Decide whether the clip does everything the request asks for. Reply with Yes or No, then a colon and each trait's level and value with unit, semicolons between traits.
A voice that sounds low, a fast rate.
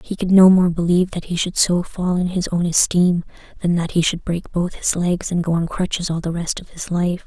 No: medium, 175 Hz; fast, 265 wpm